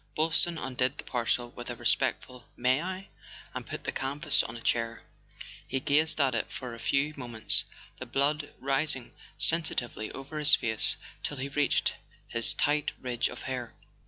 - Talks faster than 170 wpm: No, average, 165 wpm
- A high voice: No, low, 135 Hz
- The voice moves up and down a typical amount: Yes, average, 3.5 semitones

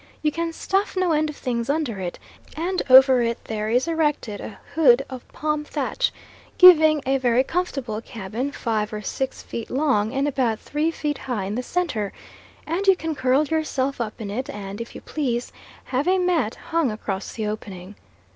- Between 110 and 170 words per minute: No, average, 185 wpm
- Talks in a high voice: Yes, very high, 265 Hz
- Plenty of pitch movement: Yes, wide, 5.7 semitones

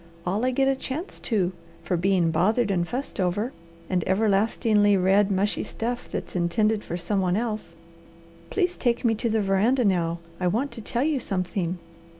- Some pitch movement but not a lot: Yes, average, 4.4 semitones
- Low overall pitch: No, high, 205 Hz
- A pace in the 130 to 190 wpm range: Yes, average, 175 wpm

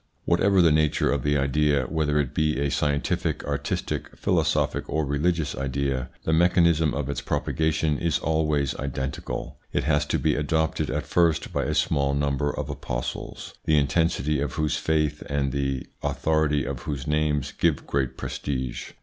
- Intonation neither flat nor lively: No, narrow, 2.1 semitones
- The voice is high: No, very low, 75 Hz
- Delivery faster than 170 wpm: No, average, 160 wpm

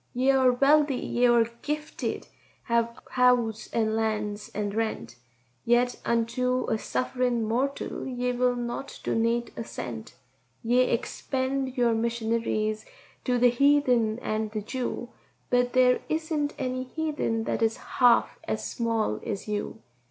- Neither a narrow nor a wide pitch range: No, narrow, 2.3 semitones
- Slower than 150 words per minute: Yes, slow, 135 wpm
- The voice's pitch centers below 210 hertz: No, high, 240 Hz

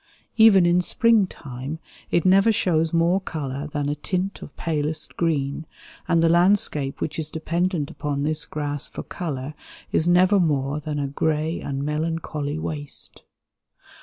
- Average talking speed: Yes, average, 150 wpm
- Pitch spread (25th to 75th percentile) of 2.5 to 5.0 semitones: Yes, average, 3.0 semitones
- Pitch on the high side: No, medium, 155 Hz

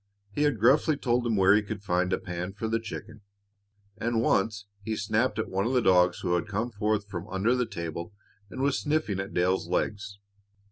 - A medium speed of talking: No, fast, 215 wpm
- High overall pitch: No, low, 105 Hz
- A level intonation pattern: No, average, 3.5 semitones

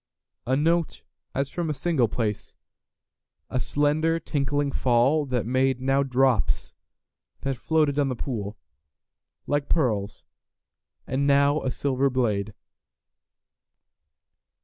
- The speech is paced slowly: Yes, slow, 100 wpm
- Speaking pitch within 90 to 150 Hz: Yes, low, 135 Hz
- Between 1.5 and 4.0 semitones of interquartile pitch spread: Yes, average, 3.2 semitones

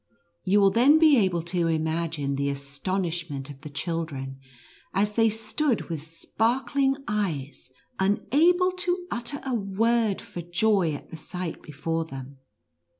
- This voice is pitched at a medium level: Yes, medium, 180 Hz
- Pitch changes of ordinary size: No, wide, 6.5 semitones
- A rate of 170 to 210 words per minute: No, average, 145 wpm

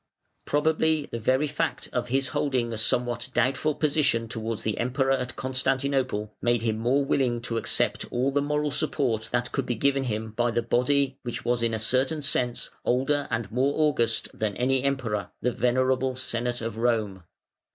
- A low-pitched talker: Yes, low, 125 Hz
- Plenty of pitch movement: No, average, 2.8 semitones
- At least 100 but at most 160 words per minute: No, average, 175 wpm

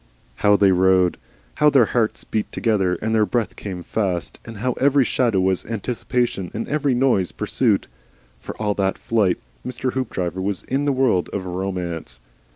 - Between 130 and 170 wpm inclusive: Yes, average, 165 wpm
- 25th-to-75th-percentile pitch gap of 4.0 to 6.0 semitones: Yes, average, 4.8 semitones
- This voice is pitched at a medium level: No, low, 105 Hz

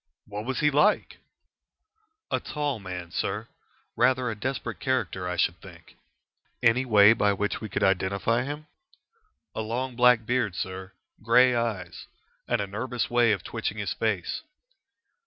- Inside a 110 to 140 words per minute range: No, average, 150 wpm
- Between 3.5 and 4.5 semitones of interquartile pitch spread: Yes, average, 4.2 semitones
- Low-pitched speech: Yes, low, 115 Hz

